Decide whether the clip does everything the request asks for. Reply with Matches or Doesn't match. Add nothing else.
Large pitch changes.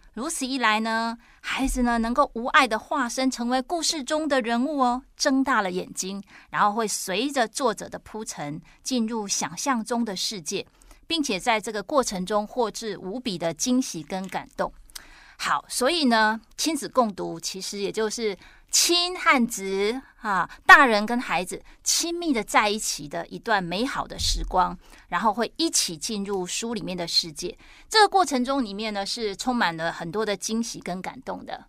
Doesn't match